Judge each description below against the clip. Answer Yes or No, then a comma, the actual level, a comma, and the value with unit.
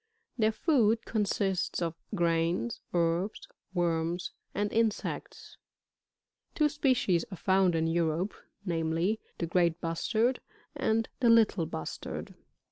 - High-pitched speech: No, medium, 180 Hz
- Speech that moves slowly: Yes, slow, 110 wpm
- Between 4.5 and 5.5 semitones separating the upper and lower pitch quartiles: Yes, average, 4.8 semitones